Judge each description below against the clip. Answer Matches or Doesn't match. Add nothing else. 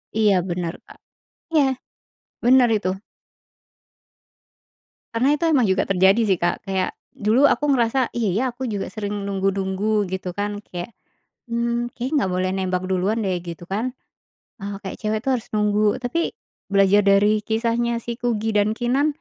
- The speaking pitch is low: Doesn't match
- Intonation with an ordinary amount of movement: Matches